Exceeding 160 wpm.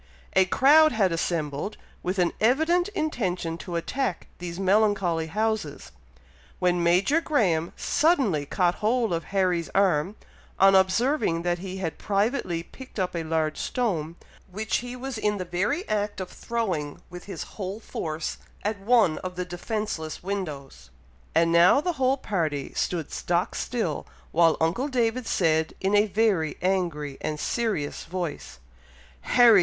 No: average, 145 wpm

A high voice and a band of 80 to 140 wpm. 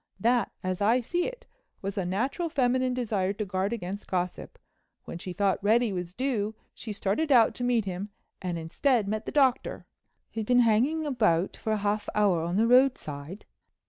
No: high, 215 Hz; average, 175 wpm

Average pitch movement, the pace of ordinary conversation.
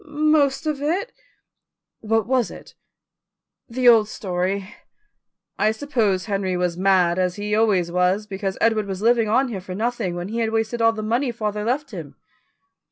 Yes: average, 3.8 semitones; average, 165 wpm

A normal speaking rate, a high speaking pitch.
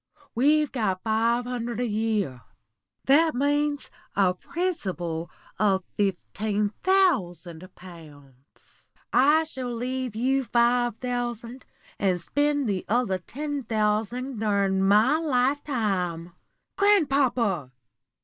No: slow, 100 wpm; high, 235 Hz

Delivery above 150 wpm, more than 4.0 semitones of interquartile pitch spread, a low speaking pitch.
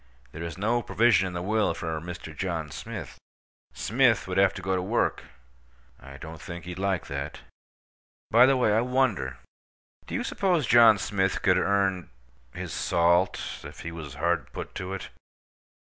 Yes: average, 165 wpm; average, 4.7 semitones; very low, 95 Hz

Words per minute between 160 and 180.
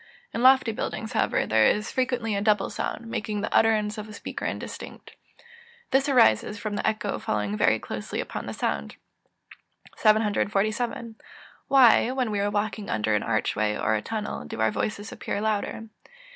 Yes: average, 170 wpm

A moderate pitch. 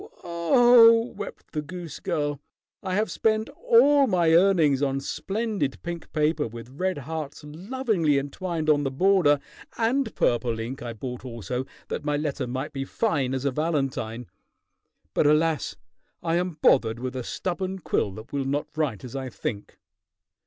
Yes: medium, 150 Hz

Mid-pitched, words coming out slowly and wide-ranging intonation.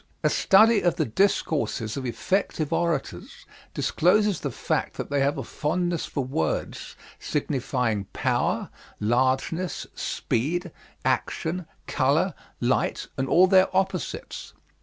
Yes: medium, 155 Hz; slow, 115 wpm; wide, 5.7 semitones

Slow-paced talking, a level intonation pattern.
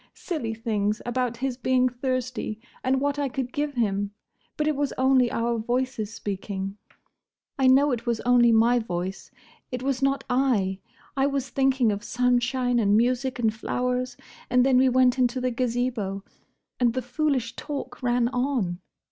No: average, 165 wpm; narrow, 2.2 semitones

